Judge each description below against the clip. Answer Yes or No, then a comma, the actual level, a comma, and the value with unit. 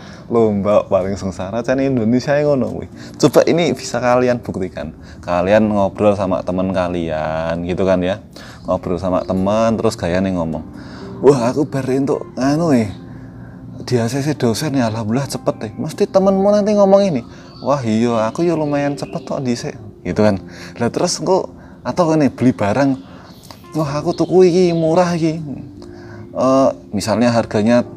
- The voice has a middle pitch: No, low, 115 Hz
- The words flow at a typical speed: No, fast, 150 wpm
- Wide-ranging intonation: Yes, wide, 7.3 semitones